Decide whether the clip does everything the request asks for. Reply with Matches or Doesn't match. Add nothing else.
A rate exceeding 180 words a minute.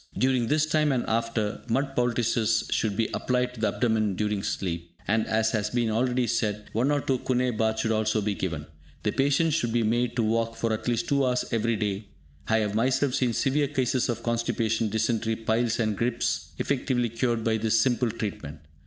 Matches